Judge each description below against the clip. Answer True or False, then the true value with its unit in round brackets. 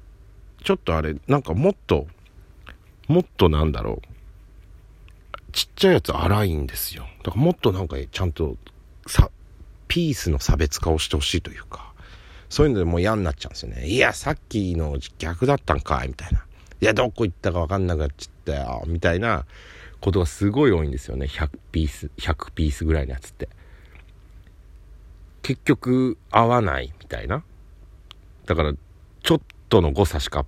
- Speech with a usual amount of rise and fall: True (4.3 semitones)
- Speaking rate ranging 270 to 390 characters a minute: True (345 characters per minute)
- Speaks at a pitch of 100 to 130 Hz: False (90 Hz)